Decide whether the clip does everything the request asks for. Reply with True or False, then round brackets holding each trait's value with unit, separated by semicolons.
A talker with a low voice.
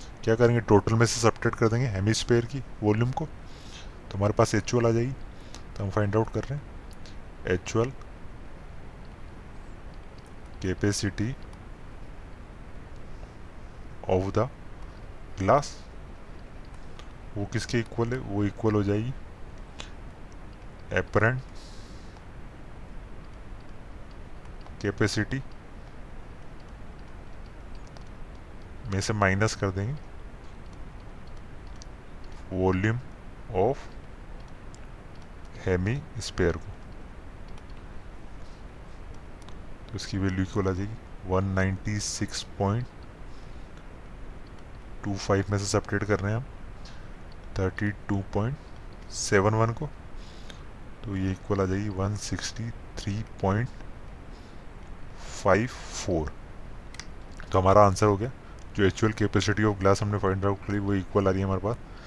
True (100 Hz)